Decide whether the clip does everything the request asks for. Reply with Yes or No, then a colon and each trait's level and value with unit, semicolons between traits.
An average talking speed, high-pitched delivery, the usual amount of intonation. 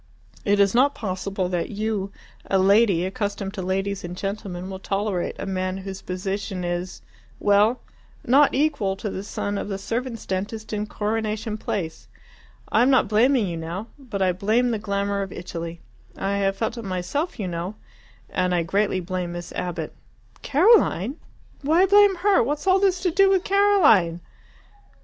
Yes: average, 170 wpm; high, 200 Hz; average, 4.1 semitones